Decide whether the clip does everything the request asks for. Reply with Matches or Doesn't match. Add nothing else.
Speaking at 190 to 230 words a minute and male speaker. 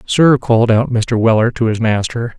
Matches